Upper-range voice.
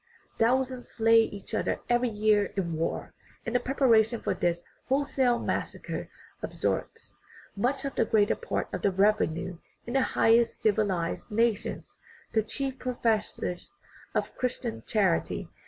Yes: high, 225 Hz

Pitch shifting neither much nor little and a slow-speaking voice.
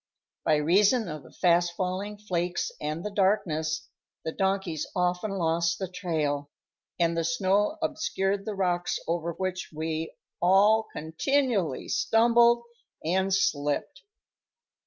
Yes: average, 3.6 semitones; slow, 120 wpm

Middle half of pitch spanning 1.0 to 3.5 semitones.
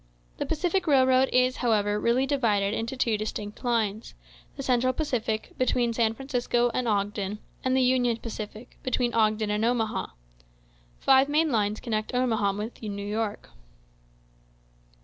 Yes: average, 3.1 semitones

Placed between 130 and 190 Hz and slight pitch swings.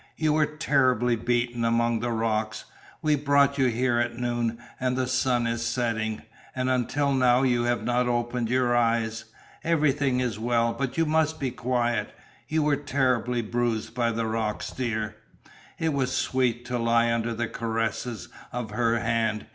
No: low, 120 Hz; narrow, 1.9 semitones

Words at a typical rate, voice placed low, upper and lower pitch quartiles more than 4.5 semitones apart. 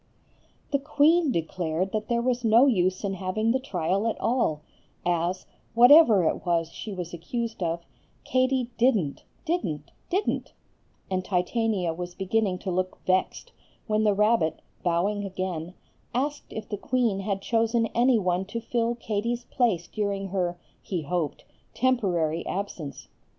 No: average, 145 wpm; high, 200 Hz; average, 4.9 semitones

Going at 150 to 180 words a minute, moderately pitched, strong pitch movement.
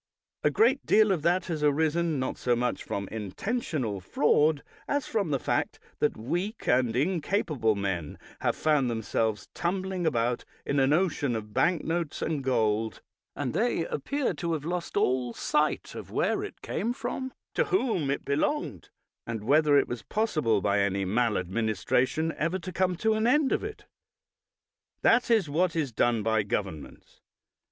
Yes: average, 160 wpm; medium, 145 Hz; wide, 8.2 semitones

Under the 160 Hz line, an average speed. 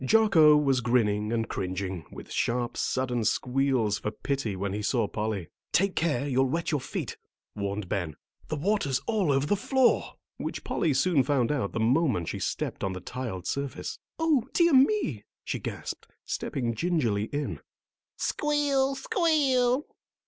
Yes: low, 135 Hz; average, 155 wpm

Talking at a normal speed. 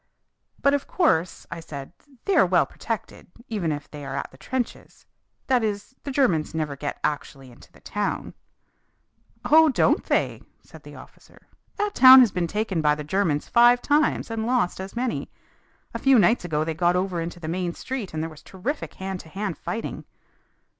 Yes: average, 190 wpm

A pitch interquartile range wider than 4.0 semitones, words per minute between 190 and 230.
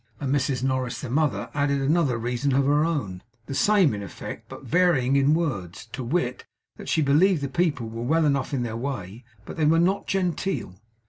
Yes: average, 4.6 semitones; average, 195 wpm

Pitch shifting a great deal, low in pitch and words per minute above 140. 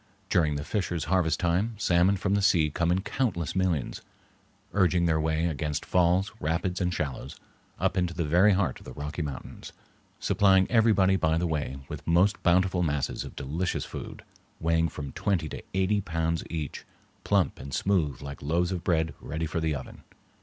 No: average, 3.2 semitones; very low, 85 Hz; average, 175 wpm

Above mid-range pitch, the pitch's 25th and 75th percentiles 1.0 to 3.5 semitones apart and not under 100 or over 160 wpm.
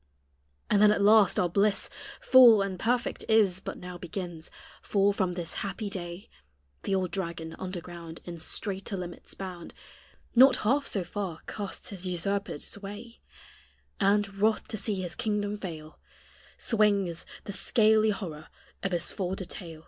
Yes: high, 195 Hz; average, 3.0 semitones; average, 150 wpm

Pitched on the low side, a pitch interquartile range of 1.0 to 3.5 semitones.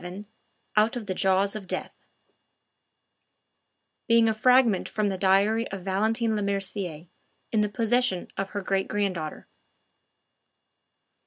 No: high, 200 Hz; narrow, 2.6 semitones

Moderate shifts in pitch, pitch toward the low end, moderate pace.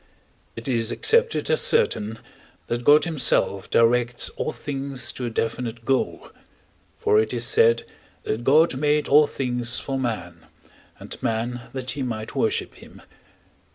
Yes: average, 3.3 semitones; low, 125 Hz; average, 145 wpm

